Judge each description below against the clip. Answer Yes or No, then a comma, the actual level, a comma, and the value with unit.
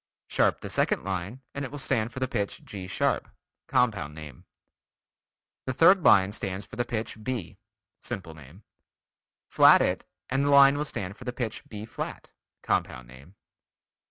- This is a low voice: Yes, low, 105 Hz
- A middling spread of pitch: No, wide, 5.7 semitones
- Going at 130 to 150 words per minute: No, average, 165 wpm